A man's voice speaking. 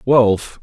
Yes: male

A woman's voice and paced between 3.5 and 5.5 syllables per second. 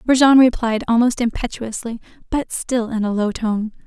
Yes: female; 4.9 syllables/s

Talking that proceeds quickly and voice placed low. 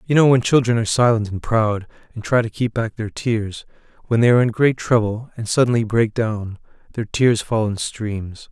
Yes: fast, 210 wpm; low, 110 Hz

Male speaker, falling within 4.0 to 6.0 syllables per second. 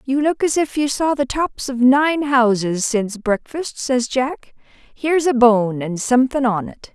No: female; 4.3 syllables/s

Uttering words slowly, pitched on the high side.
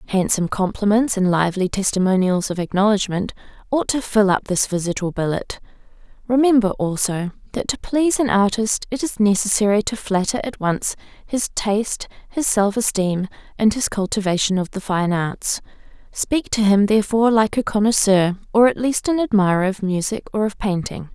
No: average, 165 wpm; high, 205 Hz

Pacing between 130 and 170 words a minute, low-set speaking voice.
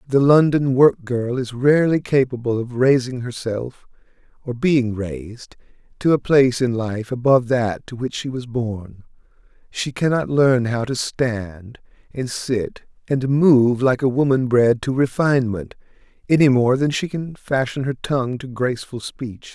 Yes: average, 160 wpm; low, 125 Hz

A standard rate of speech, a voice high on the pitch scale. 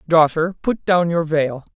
No: average, 170 wpm; medium, 165 Hz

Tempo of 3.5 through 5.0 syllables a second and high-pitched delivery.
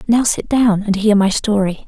Yes: 4.6 syllables/s; high, 210 Hz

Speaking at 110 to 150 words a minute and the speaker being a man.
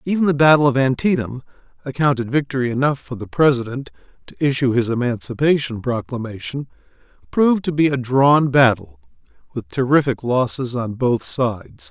Yes: average, 140 wpm; male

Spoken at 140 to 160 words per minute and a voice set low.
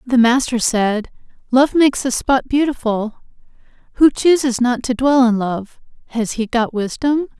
No: average, 155 wpm; very high, 250 Hz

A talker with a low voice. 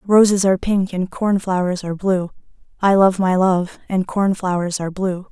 No: medium, 185 Hz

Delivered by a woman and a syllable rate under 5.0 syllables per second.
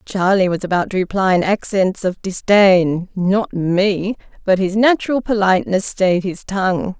Yes: female; 4.5 syllables/s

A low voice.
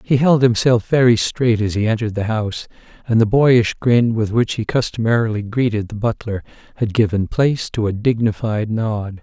Yes: low, 115 Hz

